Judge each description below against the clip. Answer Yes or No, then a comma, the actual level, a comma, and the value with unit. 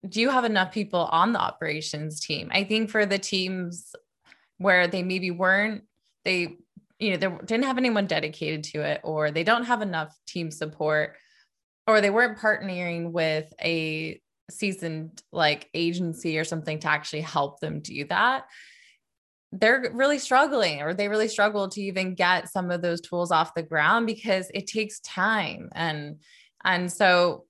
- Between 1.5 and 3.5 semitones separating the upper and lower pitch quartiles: No, average, 4.5 semitones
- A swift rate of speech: No, average, 165 wpm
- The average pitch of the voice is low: No, medium, 180 Hz